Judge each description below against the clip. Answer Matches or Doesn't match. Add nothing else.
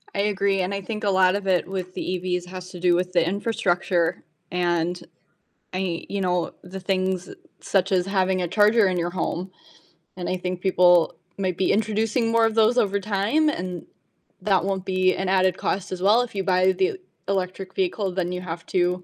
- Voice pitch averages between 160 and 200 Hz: Matches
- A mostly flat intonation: Matches